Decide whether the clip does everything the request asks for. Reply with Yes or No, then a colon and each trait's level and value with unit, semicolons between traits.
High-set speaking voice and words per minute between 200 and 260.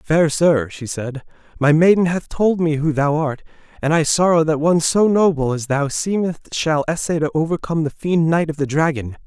No: medium, 155 Hz; fast, 205 wpm